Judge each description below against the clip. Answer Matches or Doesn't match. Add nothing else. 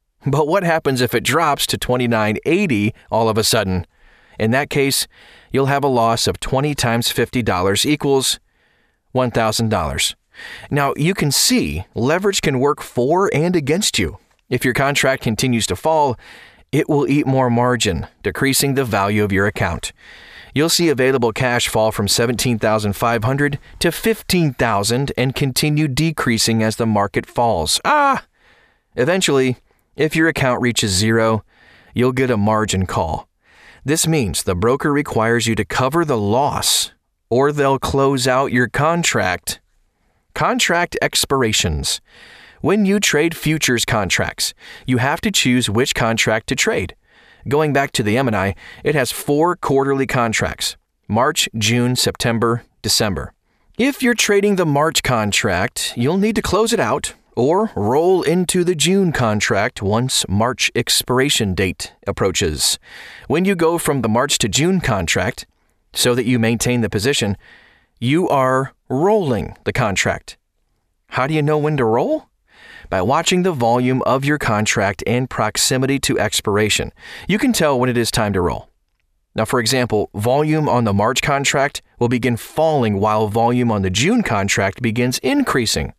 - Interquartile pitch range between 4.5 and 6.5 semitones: Matches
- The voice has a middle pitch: Doesn't match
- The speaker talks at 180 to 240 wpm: Doesn't match